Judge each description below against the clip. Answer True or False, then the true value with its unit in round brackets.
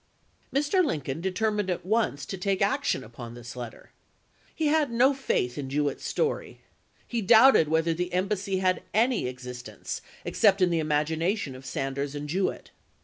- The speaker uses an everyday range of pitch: False (7.7 semitones)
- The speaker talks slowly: False (165 wpm)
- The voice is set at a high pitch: False (180 Hz)